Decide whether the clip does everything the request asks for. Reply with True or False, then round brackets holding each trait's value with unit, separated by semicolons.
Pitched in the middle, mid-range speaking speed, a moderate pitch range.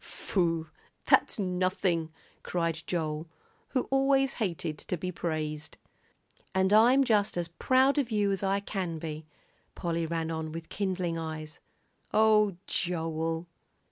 False (175 Hz; 130 wpm; 4.0 semitones)